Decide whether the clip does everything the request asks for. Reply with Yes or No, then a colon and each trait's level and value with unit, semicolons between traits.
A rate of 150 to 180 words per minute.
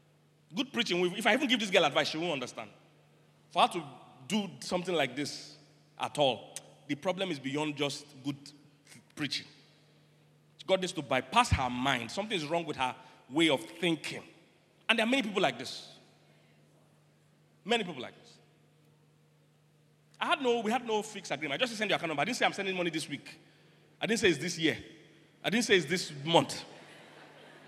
No: average, 195 wpm